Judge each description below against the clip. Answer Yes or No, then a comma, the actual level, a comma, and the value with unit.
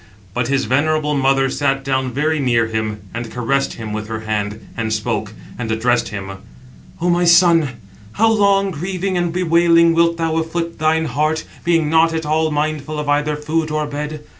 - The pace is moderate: Yes, average, 180 wpm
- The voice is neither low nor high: Yes, medium, 150 Hz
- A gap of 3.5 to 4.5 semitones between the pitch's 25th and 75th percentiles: No, average, 5.1 semitones